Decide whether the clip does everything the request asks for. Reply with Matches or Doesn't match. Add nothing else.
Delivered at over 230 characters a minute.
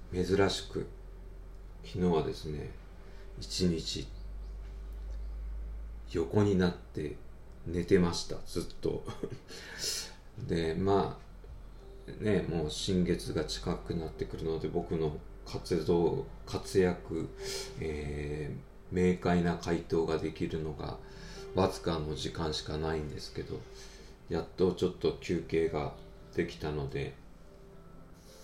Doesn't match